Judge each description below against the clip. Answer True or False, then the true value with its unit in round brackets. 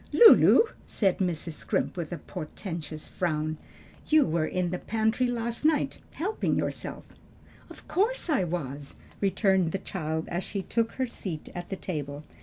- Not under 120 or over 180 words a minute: True (155 wpm)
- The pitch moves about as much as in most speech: False (6.3 semitones)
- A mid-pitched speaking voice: True (180 Hz)